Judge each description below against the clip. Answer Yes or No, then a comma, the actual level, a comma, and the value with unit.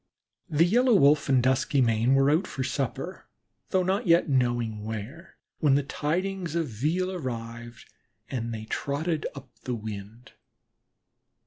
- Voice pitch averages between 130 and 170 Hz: Yes, low, 135 Hz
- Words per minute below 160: Yes, slow, 135 wpm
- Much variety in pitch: Yes, wide, 6.1 semitones